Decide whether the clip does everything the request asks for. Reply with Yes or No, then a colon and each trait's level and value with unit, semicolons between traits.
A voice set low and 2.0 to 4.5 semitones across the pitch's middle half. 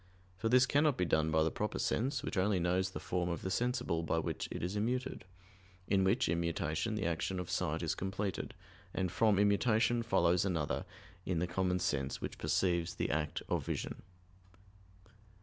Yes: very low, 90 Hz; average, 3.9 semitones